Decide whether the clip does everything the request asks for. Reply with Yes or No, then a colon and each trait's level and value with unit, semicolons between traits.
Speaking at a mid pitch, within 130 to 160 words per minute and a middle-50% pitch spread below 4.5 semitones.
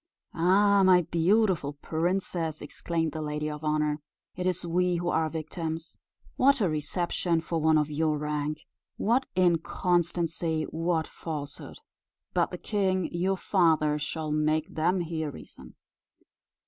Yes: medium, 165 Hz; slow, 135 wpm; average, 2.7 semitones